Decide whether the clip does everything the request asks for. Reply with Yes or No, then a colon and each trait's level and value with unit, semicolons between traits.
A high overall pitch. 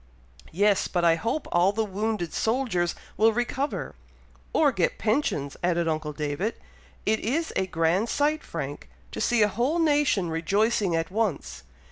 Yes: high, 205 Hz